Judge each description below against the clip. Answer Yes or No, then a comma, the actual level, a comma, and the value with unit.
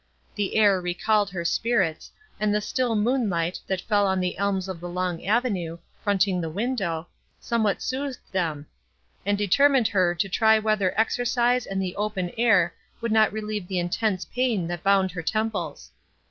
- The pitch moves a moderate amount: Yes, average, 3.6 semitones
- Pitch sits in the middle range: No, high, 200 Hz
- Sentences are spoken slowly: No, average, 165 wpm